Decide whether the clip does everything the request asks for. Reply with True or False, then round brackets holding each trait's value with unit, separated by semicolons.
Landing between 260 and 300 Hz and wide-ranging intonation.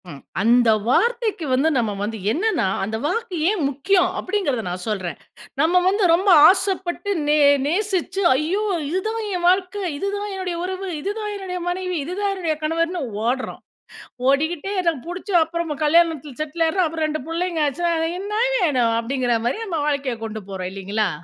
False (335 Hz; 5.9 semitones)